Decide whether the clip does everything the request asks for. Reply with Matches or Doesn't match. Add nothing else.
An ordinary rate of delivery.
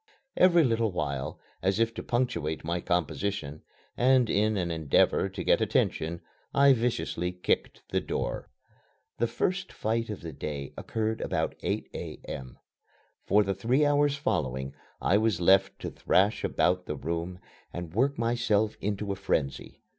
Matches